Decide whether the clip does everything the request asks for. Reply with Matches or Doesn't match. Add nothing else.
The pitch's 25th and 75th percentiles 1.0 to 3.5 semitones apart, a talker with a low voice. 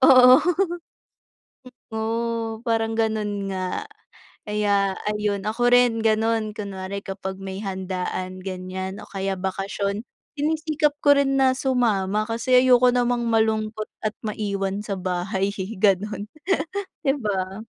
Doesn't match